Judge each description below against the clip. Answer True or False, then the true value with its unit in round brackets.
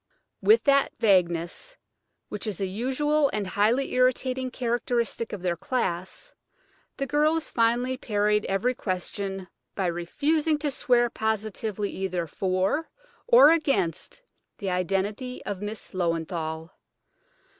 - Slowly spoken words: True (115 wpm)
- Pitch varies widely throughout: True (5.7 semitones)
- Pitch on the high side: True (215 Hz)